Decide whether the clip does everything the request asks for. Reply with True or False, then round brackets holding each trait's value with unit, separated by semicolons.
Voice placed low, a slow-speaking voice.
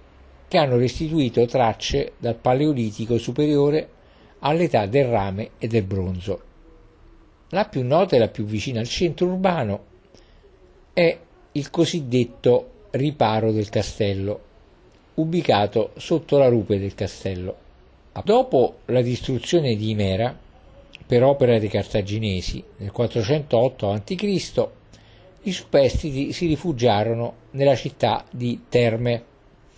True (120 Hz; 110 wpm)